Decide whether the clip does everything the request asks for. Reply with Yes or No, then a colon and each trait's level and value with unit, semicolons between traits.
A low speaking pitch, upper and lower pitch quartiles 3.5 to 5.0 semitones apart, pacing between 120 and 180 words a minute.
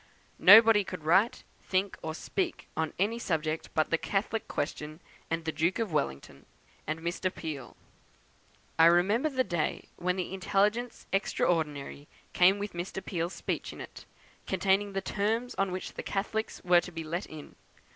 No: medium, 180 Hz; average, 3.9 semitones; average, 160 wpm